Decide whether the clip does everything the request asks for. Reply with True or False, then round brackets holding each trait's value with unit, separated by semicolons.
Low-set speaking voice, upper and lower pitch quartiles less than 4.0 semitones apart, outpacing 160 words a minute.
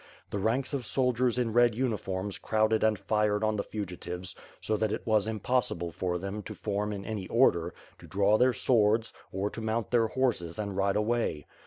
True (105 Hz; 2.8 semitones; 190 wpm)